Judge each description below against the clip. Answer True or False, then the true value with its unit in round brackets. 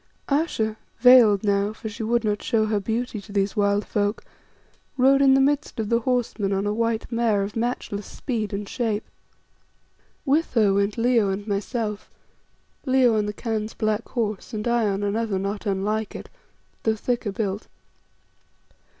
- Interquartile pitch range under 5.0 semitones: True (2.6 semitones)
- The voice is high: True (215 Hz)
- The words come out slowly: False (165 wpm)